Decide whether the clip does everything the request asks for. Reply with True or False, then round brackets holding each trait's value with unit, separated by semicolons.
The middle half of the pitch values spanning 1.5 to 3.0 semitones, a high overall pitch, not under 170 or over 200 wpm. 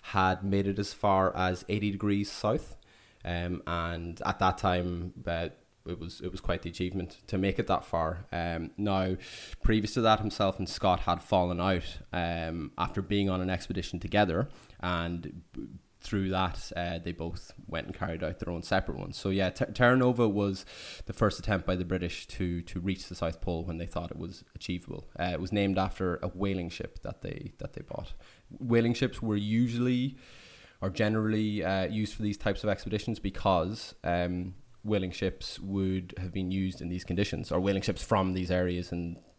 False (2.7 semitones; 95 Hz; 195 wpm)